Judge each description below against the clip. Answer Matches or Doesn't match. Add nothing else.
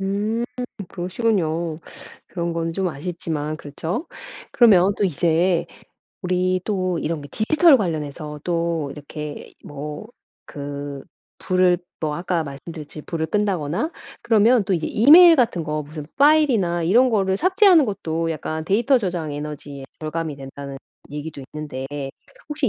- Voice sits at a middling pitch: Matches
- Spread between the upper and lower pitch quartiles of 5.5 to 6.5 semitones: Doesn't match